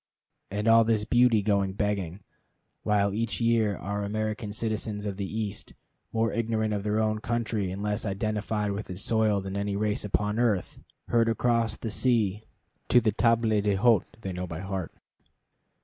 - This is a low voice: Yes, low, 105 Hz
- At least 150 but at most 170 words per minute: Yes, average, 165 wpm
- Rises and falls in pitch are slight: Yes, narrow, 2.0 semitones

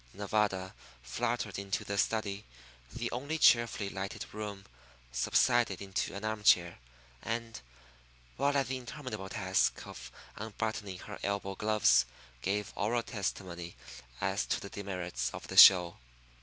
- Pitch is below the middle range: Yes, low, 100 Hz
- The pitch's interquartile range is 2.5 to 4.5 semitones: Yes, average, 3.0 semitones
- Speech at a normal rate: No, slow, 130 wpm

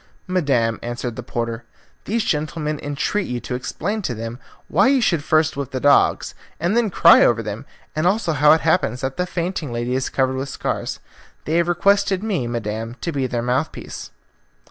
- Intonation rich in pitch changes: Yes, wide, 6.3 semitones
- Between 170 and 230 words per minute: Yes, average, 190 wpm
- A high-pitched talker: No, medium, 145 Hz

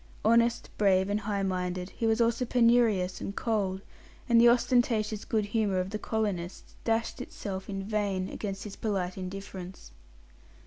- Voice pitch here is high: Yes, high, 205 Hz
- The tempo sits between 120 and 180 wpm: Yes, average, 150 wpm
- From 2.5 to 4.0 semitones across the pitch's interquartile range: Yes, average, 3.0 semitones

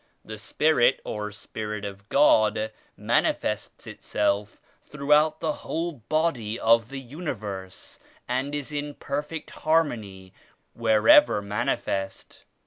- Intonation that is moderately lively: No, wide, 6.0 semitones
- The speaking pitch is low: Yes, low, 115 Hz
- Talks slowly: Yes, slow, 105 wpm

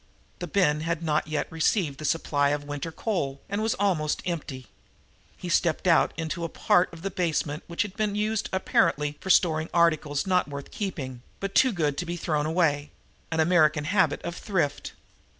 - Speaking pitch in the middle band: Yes, medium, 165 Hz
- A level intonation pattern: No, average, 3.7 semitones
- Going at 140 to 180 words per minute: No, average, 190 wpm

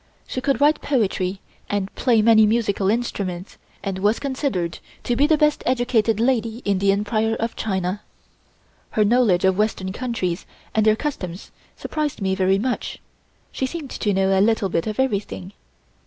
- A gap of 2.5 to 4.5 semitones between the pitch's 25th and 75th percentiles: Yes, average, 4.2 semitones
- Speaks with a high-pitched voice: Yes, high, 215 Hz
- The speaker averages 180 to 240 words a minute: No, average, 165 wpm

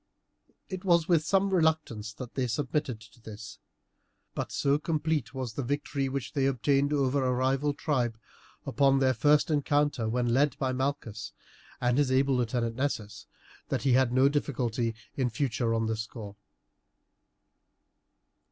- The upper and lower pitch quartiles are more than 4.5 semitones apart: No, average, 3.5 semitones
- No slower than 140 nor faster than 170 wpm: Yes, average, 150 wpm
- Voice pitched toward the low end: Yes, low, 130 Hz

